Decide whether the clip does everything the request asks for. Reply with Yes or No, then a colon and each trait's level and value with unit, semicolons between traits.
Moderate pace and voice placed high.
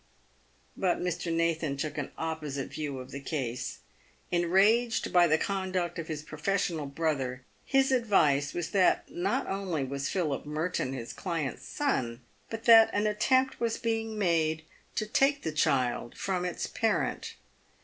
No: average, 150 wpm; medium, 170 Hz